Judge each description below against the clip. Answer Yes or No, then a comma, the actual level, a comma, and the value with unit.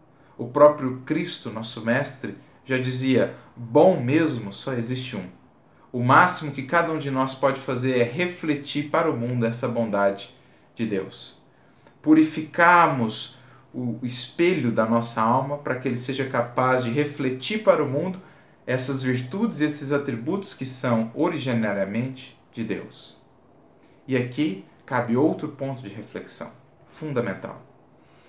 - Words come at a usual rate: Yes, average, 135 wpm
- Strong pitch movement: No, average, 3.9 semitones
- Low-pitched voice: Yes, low, 130 Hz